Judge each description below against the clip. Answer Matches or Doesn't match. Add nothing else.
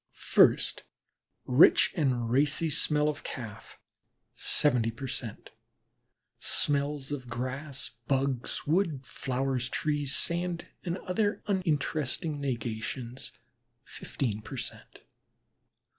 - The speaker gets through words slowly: Matches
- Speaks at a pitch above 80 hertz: Matches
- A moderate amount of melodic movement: Matches